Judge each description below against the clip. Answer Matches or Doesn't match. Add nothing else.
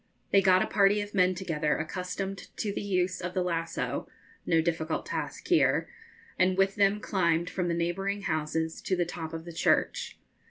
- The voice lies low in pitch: Doesn't match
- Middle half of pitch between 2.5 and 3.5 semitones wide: Matches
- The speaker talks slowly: Doesn't match